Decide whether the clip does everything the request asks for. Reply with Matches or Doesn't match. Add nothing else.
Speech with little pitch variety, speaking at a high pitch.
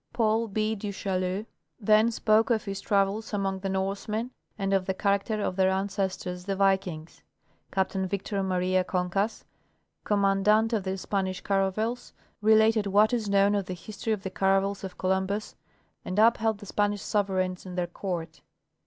Matches